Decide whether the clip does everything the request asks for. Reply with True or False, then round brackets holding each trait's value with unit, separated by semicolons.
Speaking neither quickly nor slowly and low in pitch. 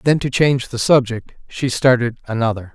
True (175 wpm; 125 Hz)